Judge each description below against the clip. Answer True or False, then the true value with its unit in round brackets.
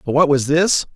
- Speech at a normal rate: False (250 wpm)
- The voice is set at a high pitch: False (150 Hz)